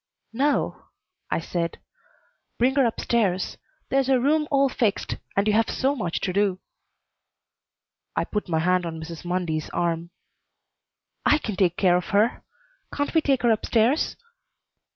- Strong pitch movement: Yes, wide, 6.9 semitones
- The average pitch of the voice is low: No, high, 210 Hz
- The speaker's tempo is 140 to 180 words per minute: Yes, average, 155 wpm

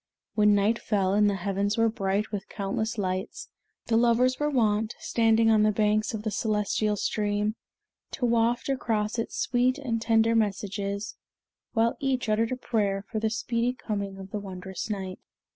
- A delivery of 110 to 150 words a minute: No, average, 170 wpm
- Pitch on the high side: Yes, high, 215 Hz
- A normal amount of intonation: No, narrow, 2.2 semitones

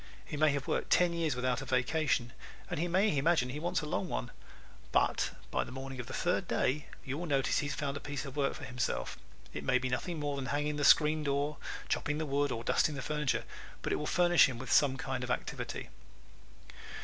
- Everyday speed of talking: No, fast, 230 wpm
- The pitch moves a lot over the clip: No, average, 2.8 semitones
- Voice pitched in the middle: Yes, medium, 145 Hz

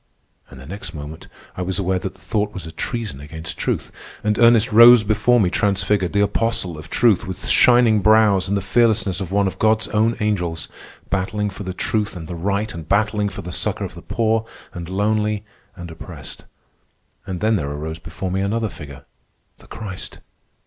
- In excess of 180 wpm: Yes, average, 190 wpm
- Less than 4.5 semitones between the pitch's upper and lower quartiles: Yes, average, 3.5 semitones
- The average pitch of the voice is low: Yes, low, 100 Hz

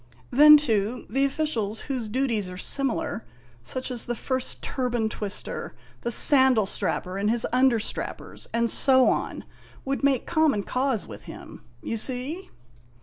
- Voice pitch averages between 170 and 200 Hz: No, very high, 250 Hz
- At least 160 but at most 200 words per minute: No, average, 145 wpm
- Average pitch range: Yes, average, 3.7 semitones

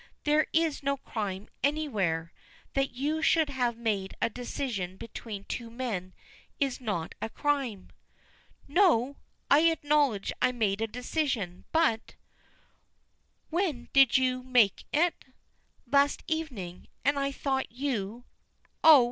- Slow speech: Yes, slow, 125 wpm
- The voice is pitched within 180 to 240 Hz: No, very high, 255 Hz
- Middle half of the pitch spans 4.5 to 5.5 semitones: Yes, average, 5.0 semitones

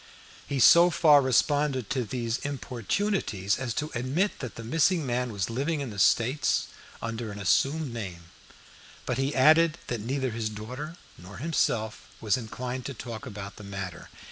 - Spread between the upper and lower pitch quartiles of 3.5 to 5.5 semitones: Yes, average, 4.8 semitones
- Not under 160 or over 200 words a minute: Yes, average, 165 wpm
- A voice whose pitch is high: No, low, 125 Hz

